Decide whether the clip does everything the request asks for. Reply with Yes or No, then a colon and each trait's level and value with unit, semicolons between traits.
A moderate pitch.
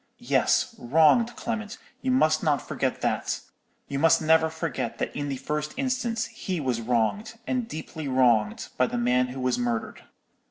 Yes: medium, 150 Hz